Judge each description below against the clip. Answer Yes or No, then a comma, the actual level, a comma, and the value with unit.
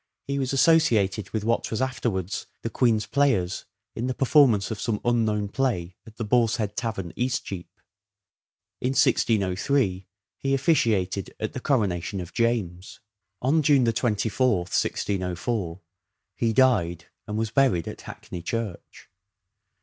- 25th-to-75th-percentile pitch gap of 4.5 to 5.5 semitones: Yes, average, 4.9 semitones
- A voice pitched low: Yes, low, 110 Hz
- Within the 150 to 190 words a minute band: No, average, 140 wpm